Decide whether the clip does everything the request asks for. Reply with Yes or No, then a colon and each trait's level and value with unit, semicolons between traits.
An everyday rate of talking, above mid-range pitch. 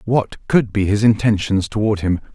No: average, 180 wpm; low, 105 Hz